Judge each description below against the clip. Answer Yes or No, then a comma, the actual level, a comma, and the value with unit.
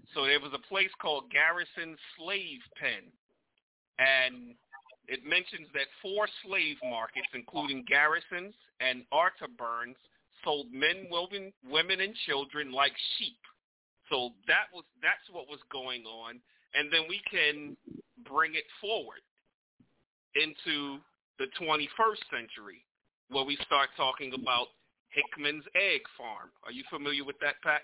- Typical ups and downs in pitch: No, wide, 5.8 semitones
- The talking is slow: Yes, slow, 130 wpm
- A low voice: No, medium, 145 Hz